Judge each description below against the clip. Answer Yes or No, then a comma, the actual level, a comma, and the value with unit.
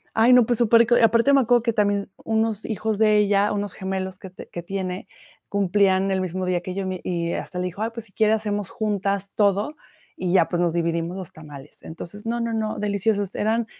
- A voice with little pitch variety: No, average, 3.0 semitones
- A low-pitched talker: No, high, 200 Hz